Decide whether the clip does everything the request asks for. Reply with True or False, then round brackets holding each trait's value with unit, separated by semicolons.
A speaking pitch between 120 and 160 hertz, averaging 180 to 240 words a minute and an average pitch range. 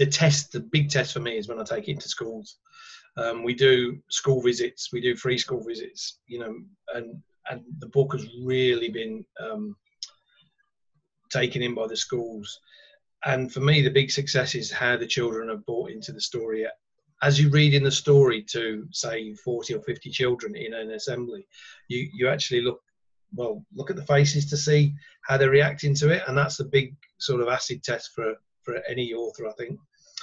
True (135 Hz; 195 wpm; 4.8 semitones)